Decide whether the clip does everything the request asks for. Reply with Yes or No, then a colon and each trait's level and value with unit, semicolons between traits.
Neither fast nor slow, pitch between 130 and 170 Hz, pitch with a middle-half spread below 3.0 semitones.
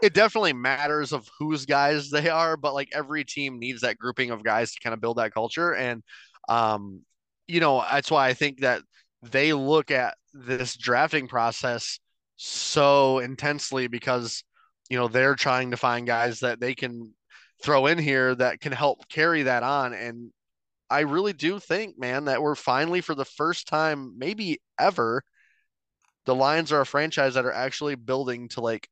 No: average, 180 wpm; low, 135 Hz; average, 3.6 semitones